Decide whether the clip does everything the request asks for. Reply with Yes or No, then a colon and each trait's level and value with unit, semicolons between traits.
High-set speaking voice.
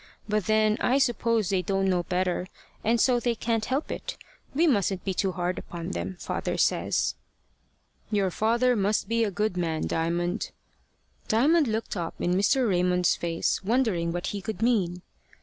Yes: high, 200 Hz